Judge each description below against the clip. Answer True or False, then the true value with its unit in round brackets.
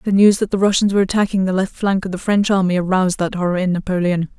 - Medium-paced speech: False (260 wpm)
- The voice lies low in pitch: False (190 Hz)